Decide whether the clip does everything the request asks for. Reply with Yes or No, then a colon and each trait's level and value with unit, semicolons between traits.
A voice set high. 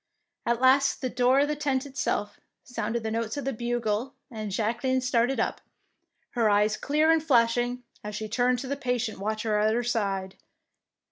Yes: high, 240 Hz